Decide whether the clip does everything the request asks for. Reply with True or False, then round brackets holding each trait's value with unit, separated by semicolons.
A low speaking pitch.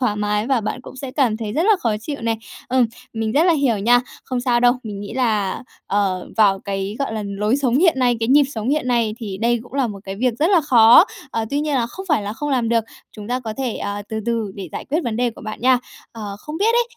False (235 Hz)